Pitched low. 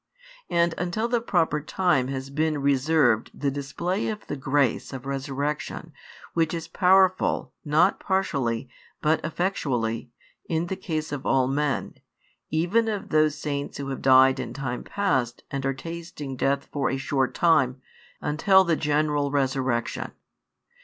No: medium, 145 Hz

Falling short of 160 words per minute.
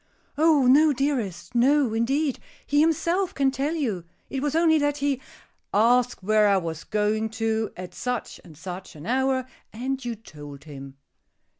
No: average, 165 wpm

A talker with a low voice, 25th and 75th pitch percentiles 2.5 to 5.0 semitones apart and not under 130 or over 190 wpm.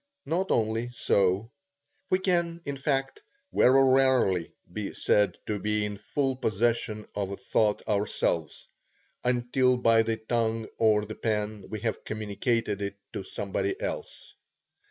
Yes: low, 110 Hz; average, 3.9 semitones; slow, 135 wpm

